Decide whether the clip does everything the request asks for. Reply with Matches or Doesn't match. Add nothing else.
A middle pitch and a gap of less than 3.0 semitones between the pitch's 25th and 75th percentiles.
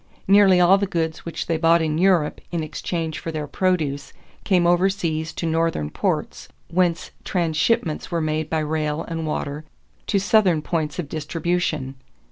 Matches